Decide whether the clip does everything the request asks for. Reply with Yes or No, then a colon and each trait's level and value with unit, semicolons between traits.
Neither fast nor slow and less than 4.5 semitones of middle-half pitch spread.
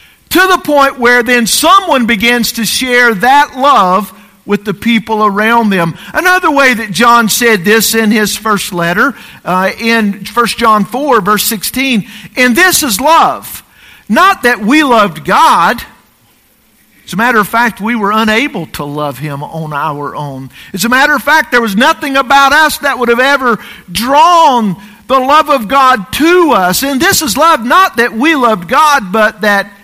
No: average, 175 wpm; average, 5.2 semitones